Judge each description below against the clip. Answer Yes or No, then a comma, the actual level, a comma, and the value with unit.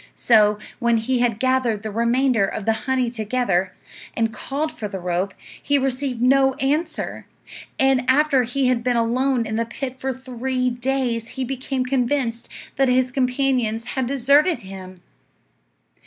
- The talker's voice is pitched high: Yes, very high, 250 Hz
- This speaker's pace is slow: No, average, 155 wpm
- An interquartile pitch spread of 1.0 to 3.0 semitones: Yes, average, 2.7 semitones